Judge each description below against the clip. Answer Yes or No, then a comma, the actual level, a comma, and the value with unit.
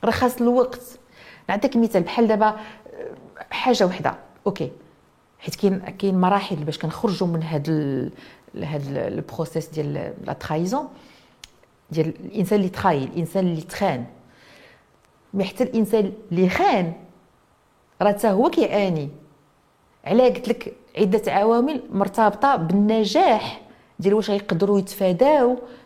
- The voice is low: No, high, 200 Hz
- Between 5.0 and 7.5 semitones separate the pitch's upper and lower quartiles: Yes, average, 5.3 semitones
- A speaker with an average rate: No, slow, 110 wpm